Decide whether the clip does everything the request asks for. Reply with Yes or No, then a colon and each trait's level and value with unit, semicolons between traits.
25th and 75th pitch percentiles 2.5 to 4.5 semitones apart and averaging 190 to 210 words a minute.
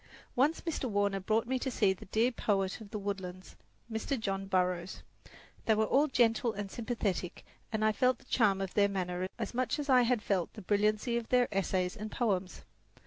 Yes: average, 3.6 semitones; average, 195 wpm